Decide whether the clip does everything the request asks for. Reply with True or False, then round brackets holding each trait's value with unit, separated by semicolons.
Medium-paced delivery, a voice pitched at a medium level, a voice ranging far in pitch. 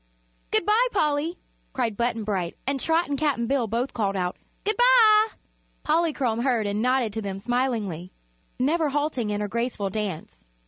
False (165 wpm; 245 Hz; 6.3 semitones)